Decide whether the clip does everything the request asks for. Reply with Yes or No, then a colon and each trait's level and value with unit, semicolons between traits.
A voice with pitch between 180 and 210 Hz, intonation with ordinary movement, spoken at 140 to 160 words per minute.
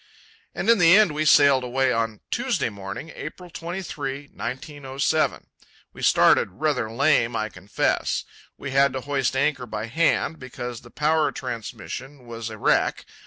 No: low, 135 Hz; average, 4.4 semitones; average, 150 wpm